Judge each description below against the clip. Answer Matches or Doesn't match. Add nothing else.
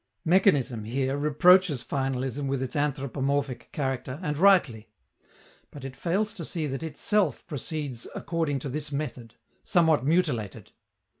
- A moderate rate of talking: Doesn't match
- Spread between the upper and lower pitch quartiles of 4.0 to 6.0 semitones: Doesn't match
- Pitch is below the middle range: Doesn't match